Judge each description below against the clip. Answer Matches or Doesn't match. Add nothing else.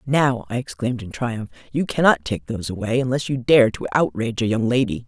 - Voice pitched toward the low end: Matches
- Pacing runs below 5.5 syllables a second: Doesn't match